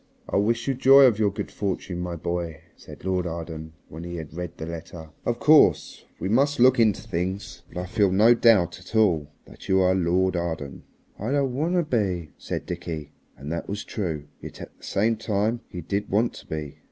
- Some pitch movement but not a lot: Yes, average, 4.9 semitones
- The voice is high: No, very low, 95 Hz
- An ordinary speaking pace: No, fast, 210 wpm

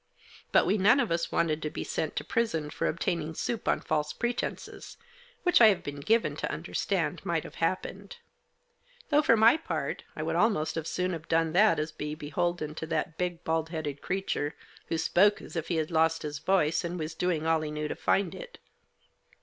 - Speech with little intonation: No, average, 3.8 semitones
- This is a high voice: No, medium, 165 Hz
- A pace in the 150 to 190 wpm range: No, fast, 205 wpm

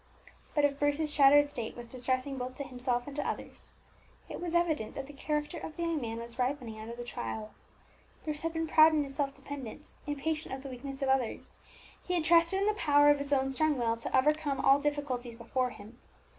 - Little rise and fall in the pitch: No, average, 3.2 semitones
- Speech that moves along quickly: Yes, fast, 215 wpm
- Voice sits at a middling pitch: No, very high, 280 Hz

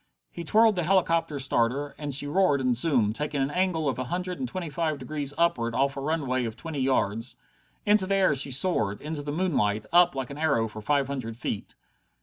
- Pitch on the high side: No, medium, 145 Hz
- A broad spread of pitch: No, average, 4.8 semitones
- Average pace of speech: No, fast, 210 wpm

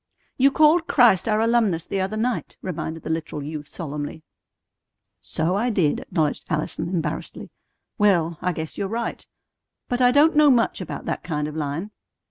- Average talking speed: Yes, average, 165 wpm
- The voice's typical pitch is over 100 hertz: Yes, medium, 185 Hz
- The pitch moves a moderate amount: No, wide, 6.9 semitones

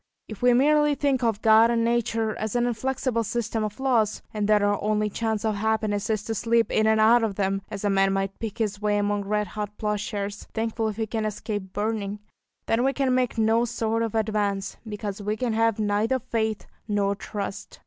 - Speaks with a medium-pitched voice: No, high, 220 Hz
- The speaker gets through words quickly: Yes, fast, 210 wpm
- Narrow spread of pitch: Yes, narrow, 1.8 semitones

